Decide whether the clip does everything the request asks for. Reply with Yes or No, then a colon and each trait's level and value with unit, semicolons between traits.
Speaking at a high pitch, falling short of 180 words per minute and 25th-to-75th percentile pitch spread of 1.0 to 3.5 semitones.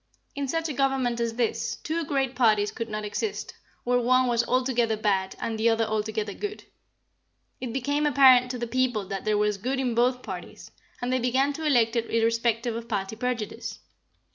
No: high, 240 Hz; average, 190 wpm; narrow, 2.6 semitones